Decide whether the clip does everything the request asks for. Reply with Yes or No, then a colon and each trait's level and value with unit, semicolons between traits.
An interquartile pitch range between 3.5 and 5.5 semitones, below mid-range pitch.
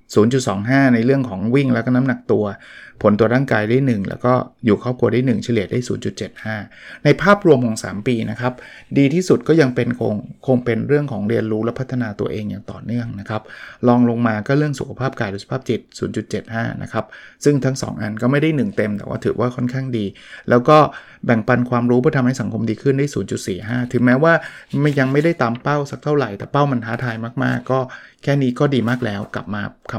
No: average, 3.1 semitones; low, 125 Hz